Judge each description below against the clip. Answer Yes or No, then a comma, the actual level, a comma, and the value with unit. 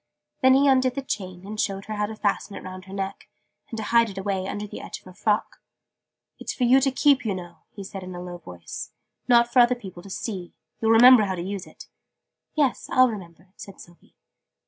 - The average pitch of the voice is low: No, high, 205 Hz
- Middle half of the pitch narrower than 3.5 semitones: No, average, 4.4 semitones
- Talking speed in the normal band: No, fast, 230 wpm